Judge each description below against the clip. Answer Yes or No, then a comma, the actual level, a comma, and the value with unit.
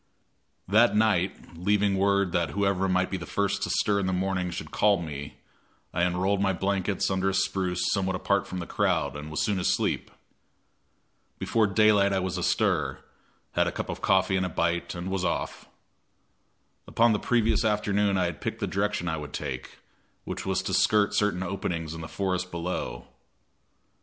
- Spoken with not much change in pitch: Yes, narrow, 2.2 semitones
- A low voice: Yes, very low, 95 Hz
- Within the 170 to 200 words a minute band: Yes, average, 180 wpm